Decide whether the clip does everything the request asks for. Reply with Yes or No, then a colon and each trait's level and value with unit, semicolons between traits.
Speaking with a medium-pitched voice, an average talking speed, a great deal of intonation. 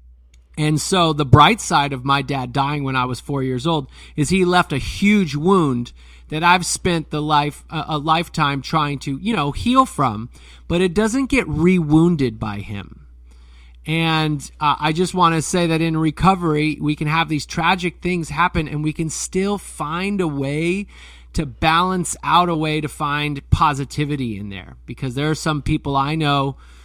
No: medium, 150 Hz; average, 185 wpm; average, 3.8 semitones